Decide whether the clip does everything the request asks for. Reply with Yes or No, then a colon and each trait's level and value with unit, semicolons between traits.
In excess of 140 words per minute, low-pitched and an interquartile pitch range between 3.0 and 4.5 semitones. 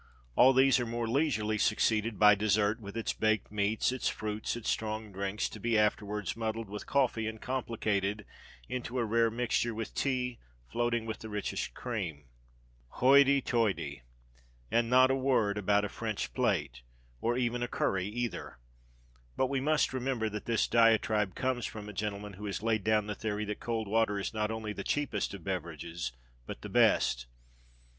No: average, 175 wpm; low, 110 Hz; narrow, 2.4 semitones